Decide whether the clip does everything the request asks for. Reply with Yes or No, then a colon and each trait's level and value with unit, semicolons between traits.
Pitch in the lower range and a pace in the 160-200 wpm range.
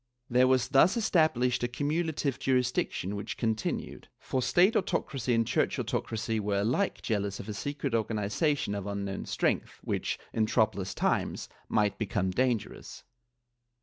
No: low, 120 Hz; average, 145 wpm